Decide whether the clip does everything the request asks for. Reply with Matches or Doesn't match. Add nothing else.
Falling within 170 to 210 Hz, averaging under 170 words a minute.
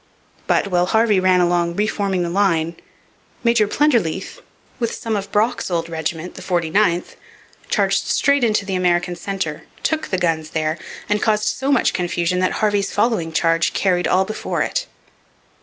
Matches